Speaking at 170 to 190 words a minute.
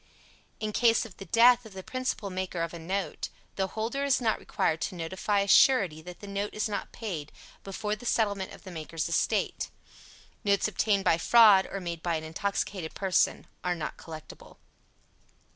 Yes: average, 180 wpm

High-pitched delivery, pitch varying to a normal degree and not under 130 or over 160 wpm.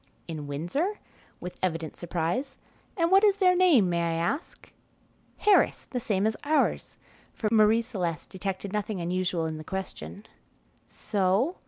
No: high, 195 Hz; wide, 7.8 semitones; average, 145 wpm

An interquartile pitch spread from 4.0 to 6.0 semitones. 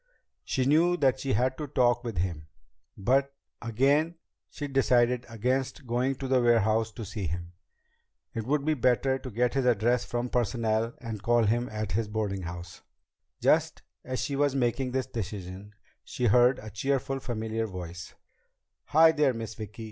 No: average, 3.5 semitones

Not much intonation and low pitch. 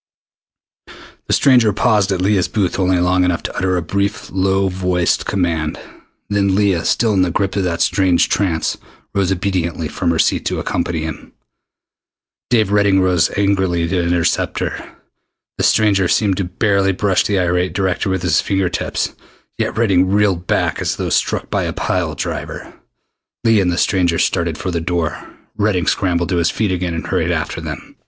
Yes: narrow, 2.2 semitones; very low, 95 Hz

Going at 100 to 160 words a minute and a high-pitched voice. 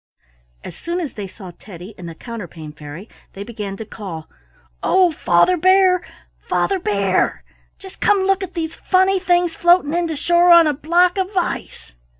No: average, 170 wpm; very high, 325 Hz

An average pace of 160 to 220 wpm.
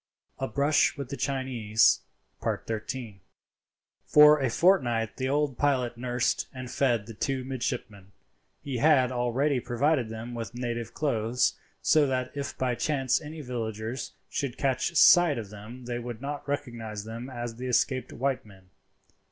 No: average, 145 wpm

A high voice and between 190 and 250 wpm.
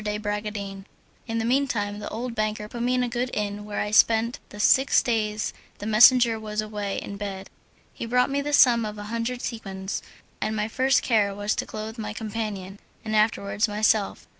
Yes: high, 215 Hz; average, 200 wpm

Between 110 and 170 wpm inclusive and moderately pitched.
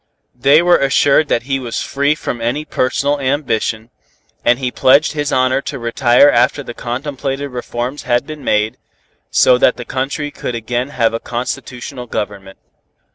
No: average, 160 wpm; low, 130 Hz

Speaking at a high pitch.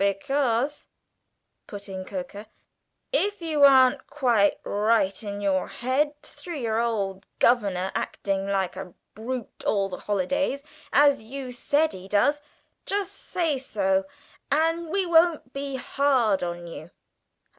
Yes: high, 240 Hz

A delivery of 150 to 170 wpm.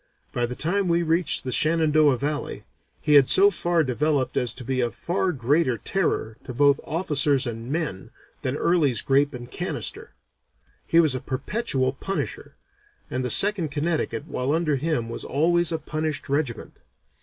Yes: average, 165 wpm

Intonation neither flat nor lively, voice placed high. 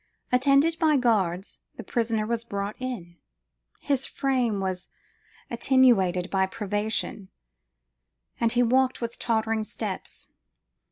Yes: average, 4.3 semitones; high, 230 Hz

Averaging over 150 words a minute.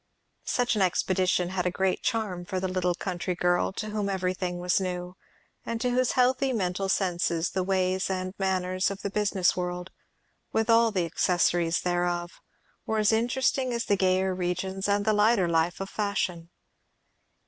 Yes: average, 170 wpm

